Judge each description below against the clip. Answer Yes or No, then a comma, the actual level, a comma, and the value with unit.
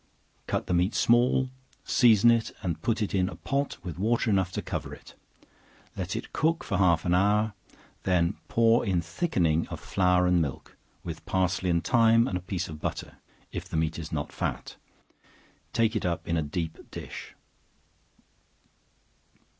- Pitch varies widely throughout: No, average, 5.0 semitones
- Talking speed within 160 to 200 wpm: Yes, average, 170 wpm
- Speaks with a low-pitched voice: Yes, very low, 95 Hz